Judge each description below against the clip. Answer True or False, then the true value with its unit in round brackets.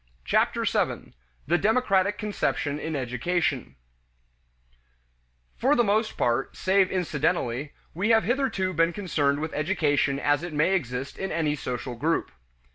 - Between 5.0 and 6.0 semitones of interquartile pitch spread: True (5.4 semitones)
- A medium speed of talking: False (130 wpm)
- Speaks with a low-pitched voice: False (160 Hz)